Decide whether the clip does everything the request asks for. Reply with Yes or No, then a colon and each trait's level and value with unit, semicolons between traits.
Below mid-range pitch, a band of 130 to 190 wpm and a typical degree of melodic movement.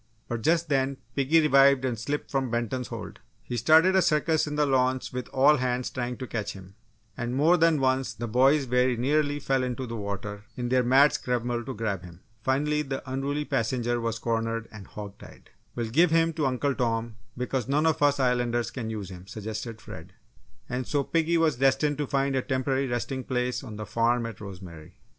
No: low, 130 Hz; average, 200 wpm; average, 3.3 semitones